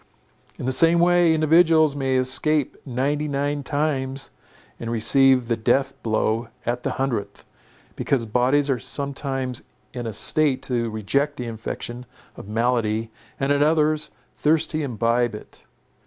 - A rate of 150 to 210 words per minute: No, average, 140 wpm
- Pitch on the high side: No, low, 135 Hz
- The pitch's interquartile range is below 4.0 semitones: Yes, average, 3.6 semitones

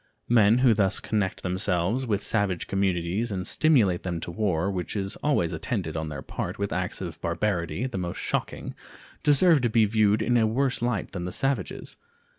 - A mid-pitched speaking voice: No, low, 100 Hz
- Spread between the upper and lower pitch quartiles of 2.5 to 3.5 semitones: No, average, 4.6 semitones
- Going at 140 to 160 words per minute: No, average, 185 wpm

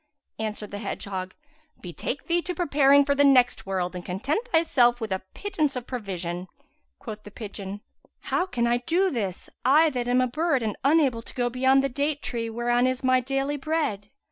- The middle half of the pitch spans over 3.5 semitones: Yes, average, 5.1 semitones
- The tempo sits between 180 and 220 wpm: Yes, average, 190 wpm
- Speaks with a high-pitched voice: Yes, very high, 250 Hz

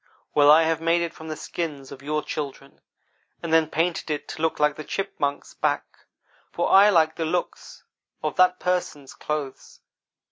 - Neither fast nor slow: Yes, average, 175 wpm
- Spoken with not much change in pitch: Yes, narrow, 2.2 semitones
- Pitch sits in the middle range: Yes, medium, 160 Hz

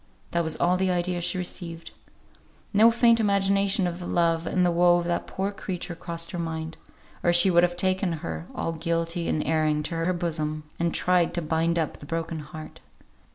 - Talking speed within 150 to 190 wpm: No, average, 200 wpm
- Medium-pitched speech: Yes, medium, 170 Hz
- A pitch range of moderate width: No, narrow, 1.8 semitones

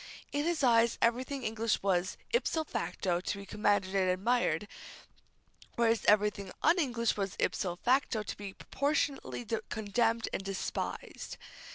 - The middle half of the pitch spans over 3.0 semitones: Yes, average, 4.1 semitones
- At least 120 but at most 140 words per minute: Yes, slow, 135 wpm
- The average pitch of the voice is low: No, high, 220 Hz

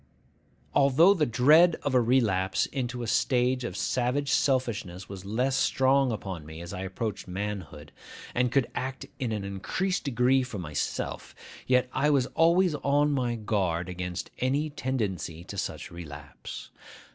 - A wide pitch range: Yes, wide, 6.1 semitones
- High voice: No, low, 120 Hz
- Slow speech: No, average, 150 wpm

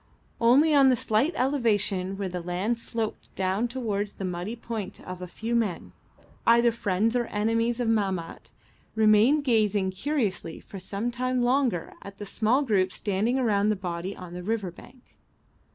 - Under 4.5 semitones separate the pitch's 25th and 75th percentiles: Yes, average, 3.9 semitones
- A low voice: No, high, 215 Hz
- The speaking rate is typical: Yes, average, 160 wpm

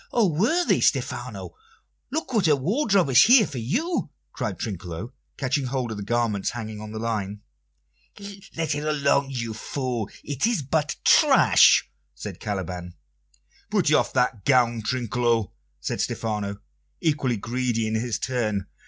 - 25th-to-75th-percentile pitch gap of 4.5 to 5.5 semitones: Yes, average, 5.2 semitones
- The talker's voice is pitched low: Yes, low, 125 Hz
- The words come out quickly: No, average, 145 wpm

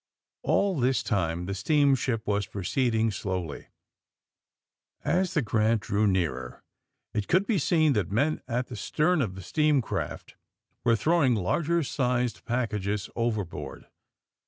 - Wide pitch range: Yes, wide, 6.2 semitones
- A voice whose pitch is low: Yes, low, 115 Hz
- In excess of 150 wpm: No, slow, 135 wpm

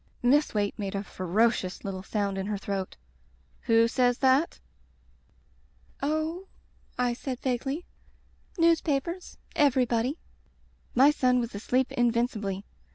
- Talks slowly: Yes, slow, 115 wpm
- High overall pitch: Yes, high, 245 Hz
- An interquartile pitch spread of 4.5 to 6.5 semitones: Yes, average, 5.1 semitones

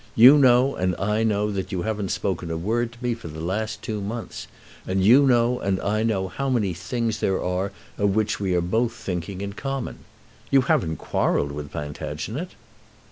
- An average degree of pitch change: Yes, average, 4.4 semitones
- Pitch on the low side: Yes, low, 105 Hz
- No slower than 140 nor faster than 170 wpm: No, average, 190 wpm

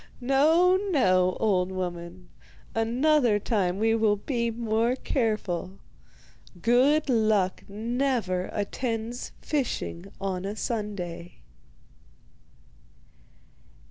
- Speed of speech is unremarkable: No, slow, 80 wpm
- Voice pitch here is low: No, high, 220 Hz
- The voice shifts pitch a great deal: No, average, 4.7 semitones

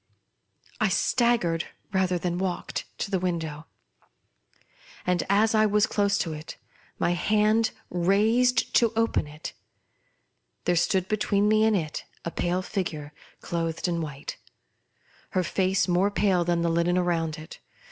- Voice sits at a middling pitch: Yes, medium, 180 Hz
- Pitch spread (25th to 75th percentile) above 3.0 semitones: Yes, average, 3.6 semitones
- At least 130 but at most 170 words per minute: Yes, average, 145 wpm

